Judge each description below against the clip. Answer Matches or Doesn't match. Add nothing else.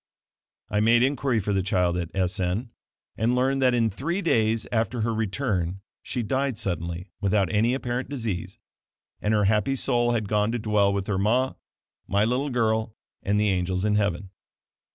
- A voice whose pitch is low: Matches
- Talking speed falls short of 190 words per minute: Matches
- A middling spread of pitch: Matches